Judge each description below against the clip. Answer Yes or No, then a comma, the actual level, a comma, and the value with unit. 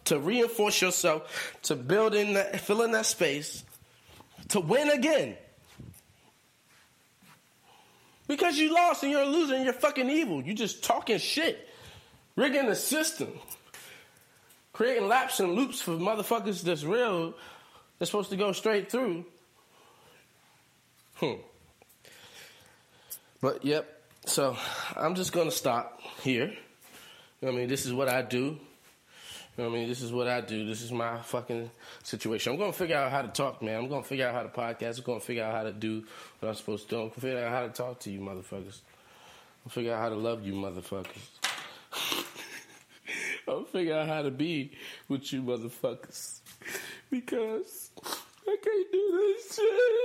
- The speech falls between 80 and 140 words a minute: No, average, 170 wpm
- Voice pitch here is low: No, medium, 160 Hz